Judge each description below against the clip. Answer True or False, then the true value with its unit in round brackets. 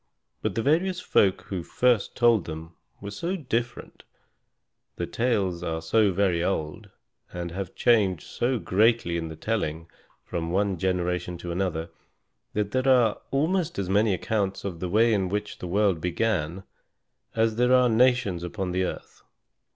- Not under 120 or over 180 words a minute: True (160 wpm)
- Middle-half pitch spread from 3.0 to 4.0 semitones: False (4.7 semitones)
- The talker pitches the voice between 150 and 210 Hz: False (100 Hz)